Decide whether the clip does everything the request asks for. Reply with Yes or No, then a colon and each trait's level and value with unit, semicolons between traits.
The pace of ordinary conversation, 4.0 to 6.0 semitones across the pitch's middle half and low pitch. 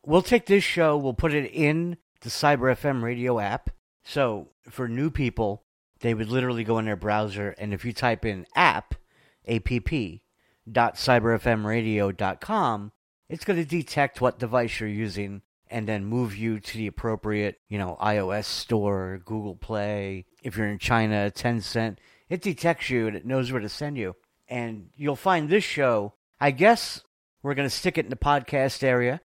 Yes: average, 170 wpm; average, 5.0 semitones; low, 115 Hz